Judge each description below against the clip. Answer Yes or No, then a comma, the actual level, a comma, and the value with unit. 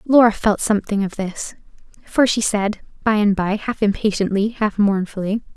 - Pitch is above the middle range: Yes, high, 210 Hz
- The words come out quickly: No, average, 160 wpm